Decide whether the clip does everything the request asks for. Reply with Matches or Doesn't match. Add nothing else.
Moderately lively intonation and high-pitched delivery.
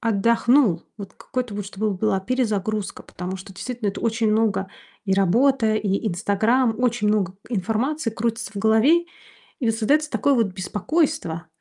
Matches